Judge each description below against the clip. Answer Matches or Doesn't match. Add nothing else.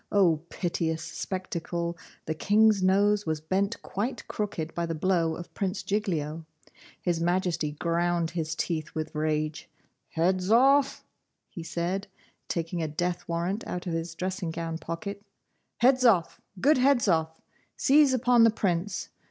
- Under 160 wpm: Matches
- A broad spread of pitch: Doesn't match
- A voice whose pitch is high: Doesn't match